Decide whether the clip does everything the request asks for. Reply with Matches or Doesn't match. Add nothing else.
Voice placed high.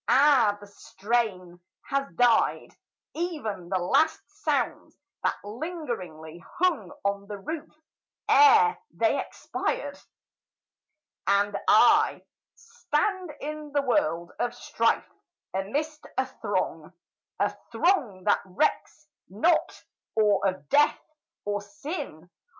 Matches